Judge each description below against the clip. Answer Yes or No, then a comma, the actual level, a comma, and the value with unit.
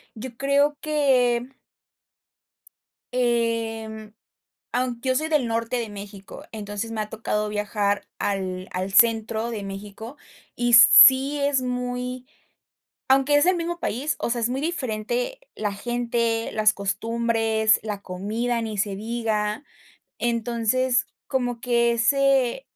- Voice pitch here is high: Yes, high, 235 Hz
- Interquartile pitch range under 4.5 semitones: Yes, average, 2.8 semitones